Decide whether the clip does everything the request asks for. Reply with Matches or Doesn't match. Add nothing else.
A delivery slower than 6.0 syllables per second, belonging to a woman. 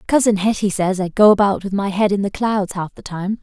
Matches